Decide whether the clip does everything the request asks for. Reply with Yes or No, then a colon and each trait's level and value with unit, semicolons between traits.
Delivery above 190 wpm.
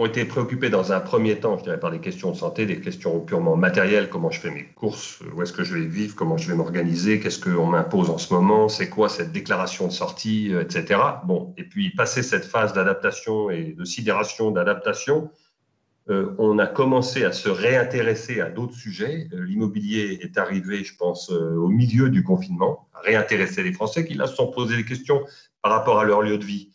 Yes: average, 215 wpm